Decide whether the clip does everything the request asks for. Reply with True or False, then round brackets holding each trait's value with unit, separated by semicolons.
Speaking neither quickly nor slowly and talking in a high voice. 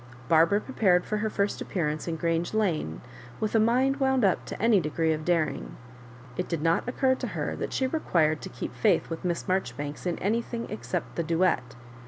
False (190 wpm; 180 Hz)